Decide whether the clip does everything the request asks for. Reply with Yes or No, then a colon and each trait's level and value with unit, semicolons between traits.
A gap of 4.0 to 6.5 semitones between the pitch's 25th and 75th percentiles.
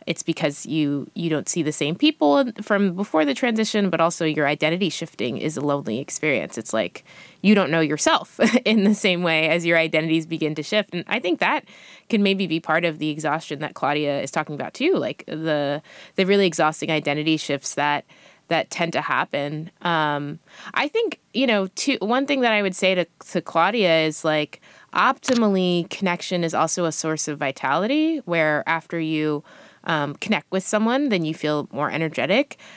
Yes: average, 4.4 semitones